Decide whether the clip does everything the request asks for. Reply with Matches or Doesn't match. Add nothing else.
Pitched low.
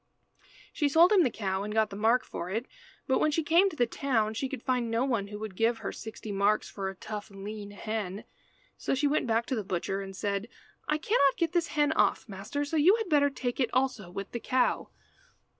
Doesn't match